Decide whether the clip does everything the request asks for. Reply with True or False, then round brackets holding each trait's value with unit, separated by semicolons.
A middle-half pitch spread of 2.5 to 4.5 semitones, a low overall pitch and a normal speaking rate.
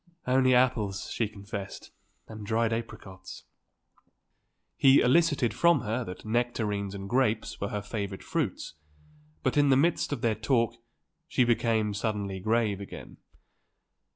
False (3.5 semitones; 110 Hz; 130 wpm)